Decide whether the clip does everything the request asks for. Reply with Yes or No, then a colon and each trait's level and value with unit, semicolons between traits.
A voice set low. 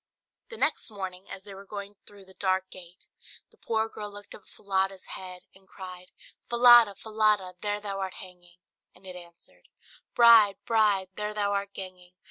No: high, 195 Hz